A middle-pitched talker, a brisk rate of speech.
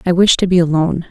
Yes: medium, 175 Hz; fast, 270 wpm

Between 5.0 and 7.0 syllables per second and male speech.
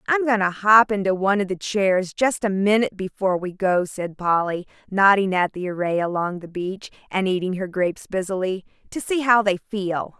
No: 5.2 syllables/s; female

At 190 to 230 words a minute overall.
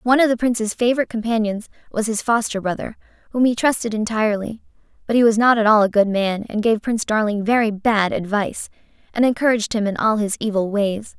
Yes: fast, 205 wpm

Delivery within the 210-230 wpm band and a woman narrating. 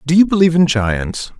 No: fast, 215 wpm; male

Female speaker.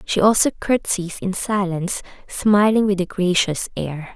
Yes: female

